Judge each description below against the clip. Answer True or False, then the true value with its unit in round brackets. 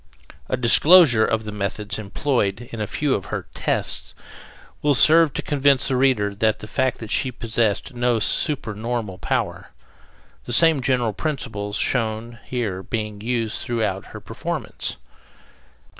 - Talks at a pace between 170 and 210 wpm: False (145 wpm)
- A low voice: True (115 Hz)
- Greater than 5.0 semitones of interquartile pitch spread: False (3.6 semitones)